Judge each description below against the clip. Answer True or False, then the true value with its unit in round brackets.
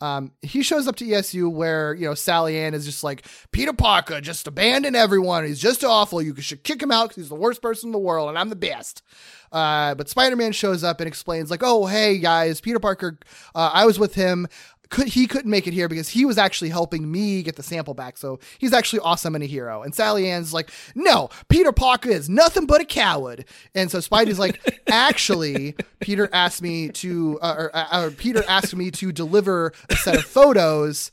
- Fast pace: True (215 wpm)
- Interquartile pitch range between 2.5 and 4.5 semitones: False (5.3 semitones)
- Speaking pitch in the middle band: True (180 Hz)